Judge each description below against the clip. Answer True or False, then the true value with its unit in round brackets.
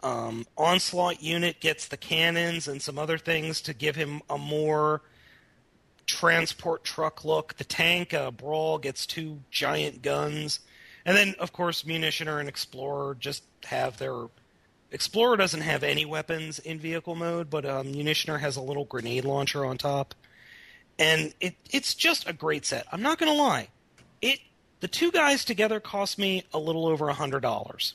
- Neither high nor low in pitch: True (155 Hz)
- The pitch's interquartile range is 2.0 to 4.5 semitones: True (2.8 semitones)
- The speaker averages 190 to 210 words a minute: False (170 wpm)